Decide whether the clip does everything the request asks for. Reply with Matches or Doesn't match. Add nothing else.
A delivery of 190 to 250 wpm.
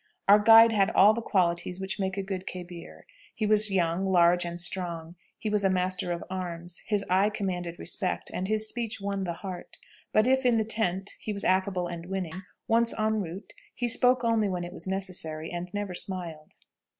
Matches